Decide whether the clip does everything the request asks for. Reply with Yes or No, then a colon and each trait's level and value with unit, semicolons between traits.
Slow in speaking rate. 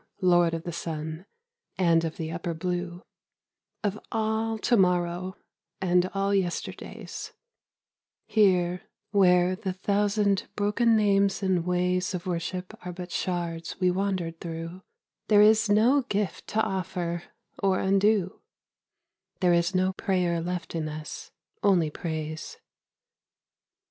Yes: slow, 125 wpm